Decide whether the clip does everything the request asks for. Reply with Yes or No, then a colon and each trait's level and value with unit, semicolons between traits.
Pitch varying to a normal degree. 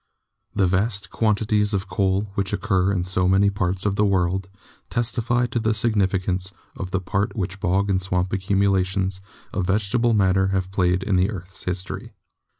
No: narrow, 1.8 semitones